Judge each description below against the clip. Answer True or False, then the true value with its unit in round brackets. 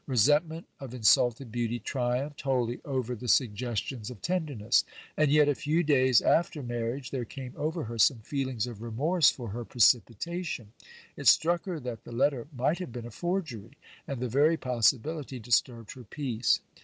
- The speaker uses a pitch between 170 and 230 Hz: False (125 Hz)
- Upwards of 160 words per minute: True (175 wpm)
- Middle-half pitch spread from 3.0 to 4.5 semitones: True (3.9 semitones)